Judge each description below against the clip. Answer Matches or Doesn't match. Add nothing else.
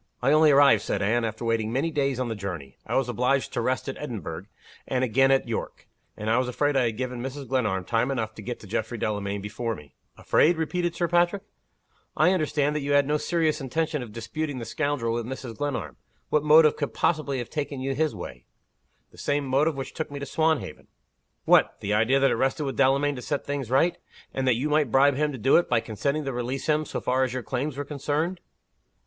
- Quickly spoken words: Matches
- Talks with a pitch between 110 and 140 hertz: Matches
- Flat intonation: Doesn't match